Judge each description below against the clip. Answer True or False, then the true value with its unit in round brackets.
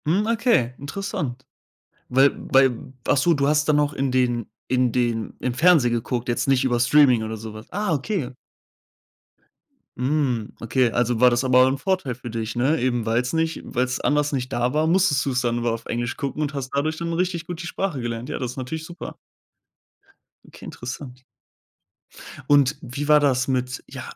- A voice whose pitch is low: True (130 Hz)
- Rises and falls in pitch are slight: False (3.7 semitones)